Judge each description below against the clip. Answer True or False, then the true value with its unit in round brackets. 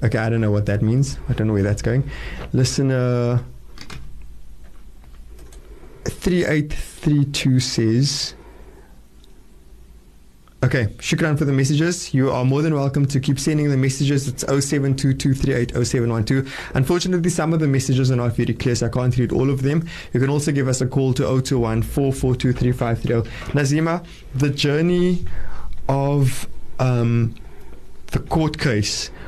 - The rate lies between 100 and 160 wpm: True (135 wpm)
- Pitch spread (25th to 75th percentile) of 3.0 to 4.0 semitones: True (3.4 semitones)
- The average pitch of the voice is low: True (130 Hz)